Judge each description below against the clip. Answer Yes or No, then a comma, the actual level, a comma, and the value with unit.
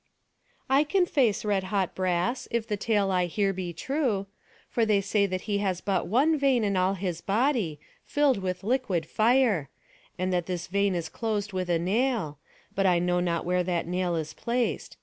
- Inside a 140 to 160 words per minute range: No, average, 190 wpm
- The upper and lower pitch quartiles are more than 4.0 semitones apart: Yes, average, 4.4 semitones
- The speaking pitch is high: Yes, high, 195 Hz